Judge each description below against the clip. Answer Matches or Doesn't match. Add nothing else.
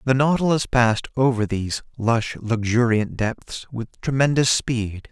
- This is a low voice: Matches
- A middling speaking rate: Doesn't match